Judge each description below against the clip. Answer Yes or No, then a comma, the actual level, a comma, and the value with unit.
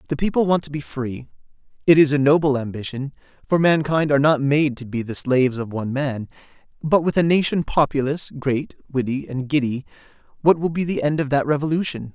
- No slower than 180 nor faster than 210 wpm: Yes, average, 200 wpm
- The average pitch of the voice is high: No, medium, 145 Hz